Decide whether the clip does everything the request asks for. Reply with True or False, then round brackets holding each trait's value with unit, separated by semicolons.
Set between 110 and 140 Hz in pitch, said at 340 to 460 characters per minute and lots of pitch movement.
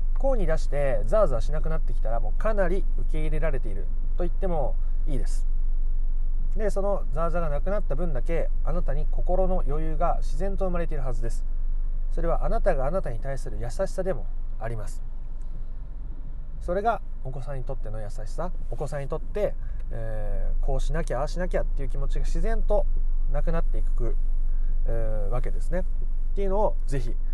True (135 Hz; 380 characters per minute; 6.2 semitones)